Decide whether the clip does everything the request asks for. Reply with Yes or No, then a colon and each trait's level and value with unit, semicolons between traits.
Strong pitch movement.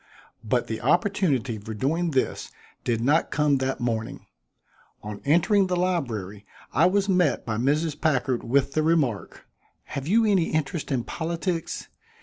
Yes: wide, 6.0 semitones